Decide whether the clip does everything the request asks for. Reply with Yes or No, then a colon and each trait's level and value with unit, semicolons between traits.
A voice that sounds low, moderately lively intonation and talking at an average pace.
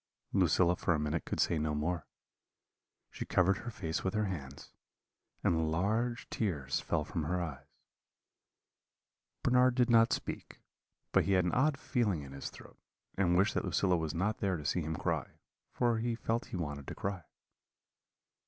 No: very low, 90 Hz; wide, 5.7 semitones; average, 170 wpm